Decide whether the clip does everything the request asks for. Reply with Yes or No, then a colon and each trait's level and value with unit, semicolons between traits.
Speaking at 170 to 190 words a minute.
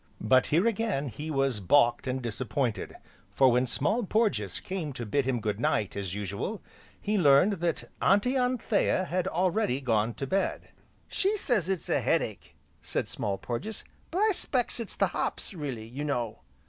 Yes: average, 175 wpm